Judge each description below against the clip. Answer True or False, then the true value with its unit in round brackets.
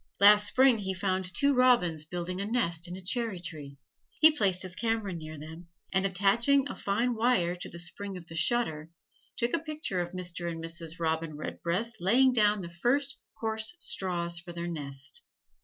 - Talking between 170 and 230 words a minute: True (175 wpm)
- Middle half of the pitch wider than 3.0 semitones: True (5.3 semitones)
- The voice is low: False (185 Hz)